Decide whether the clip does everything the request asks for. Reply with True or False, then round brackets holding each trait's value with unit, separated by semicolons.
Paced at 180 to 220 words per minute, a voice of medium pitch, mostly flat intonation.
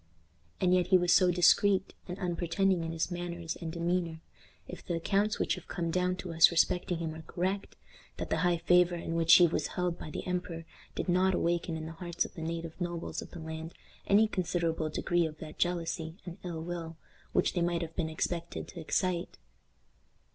True (200 wpm; 175 Hz; 1.5 semitones)